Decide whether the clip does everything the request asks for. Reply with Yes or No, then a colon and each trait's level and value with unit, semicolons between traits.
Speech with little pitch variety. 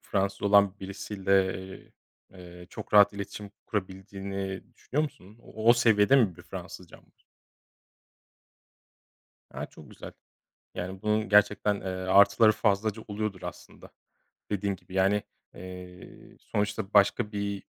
Yes: narrow, 1.6 semitones